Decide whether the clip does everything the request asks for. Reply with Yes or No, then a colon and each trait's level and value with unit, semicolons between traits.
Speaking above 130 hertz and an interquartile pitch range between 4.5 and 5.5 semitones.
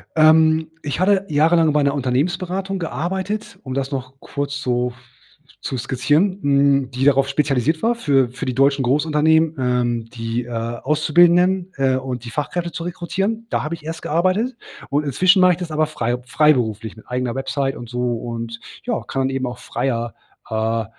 Yes: medium, 140 Hz; average, 5.1 semitones